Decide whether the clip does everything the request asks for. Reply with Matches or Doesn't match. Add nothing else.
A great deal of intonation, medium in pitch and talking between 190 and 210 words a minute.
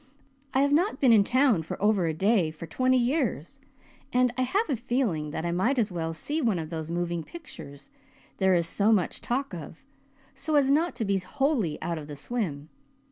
Doesn't match